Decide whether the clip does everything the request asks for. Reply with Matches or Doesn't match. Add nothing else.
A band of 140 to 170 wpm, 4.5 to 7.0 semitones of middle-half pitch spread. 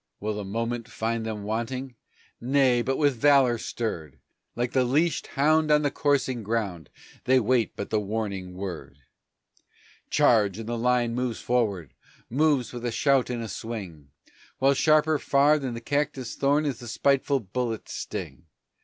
Doesn't match